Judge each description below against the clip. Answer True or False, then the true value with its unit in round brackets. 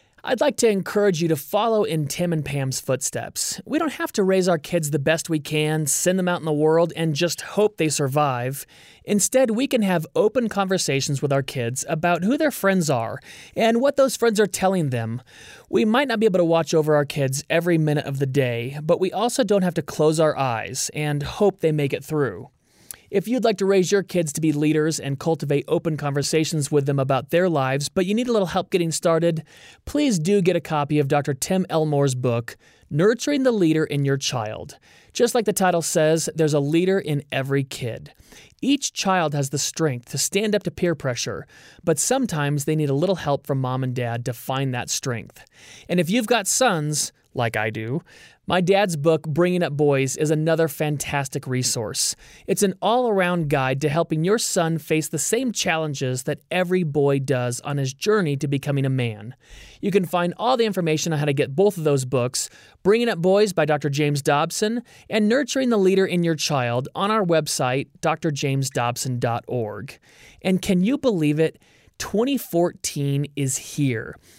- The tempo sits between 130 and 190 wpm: False (200 wpm)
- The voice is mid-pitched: True (160 Hz)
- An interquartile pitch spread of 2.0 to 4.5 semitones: False (5.2 semitones)